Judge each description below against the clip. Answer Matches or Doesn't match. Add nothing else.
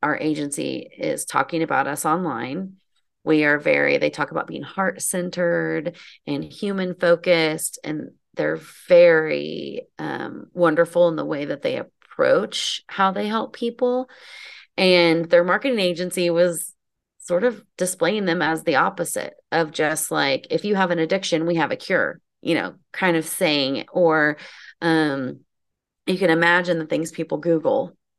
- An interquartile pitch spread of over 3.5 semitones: Doesn't match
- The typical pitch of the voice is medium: Matches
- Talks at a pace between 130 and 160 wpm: Matches